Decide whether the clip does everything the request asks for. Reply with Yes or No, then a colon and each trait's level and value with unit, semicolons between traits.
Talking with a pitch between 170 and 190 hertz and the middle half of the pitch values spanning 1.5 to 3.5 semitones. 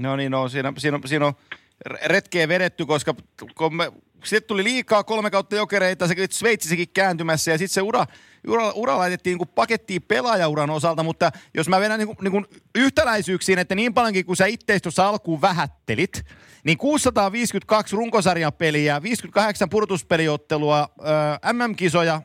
No: medium, 185 Hz; average, 4.7 semitones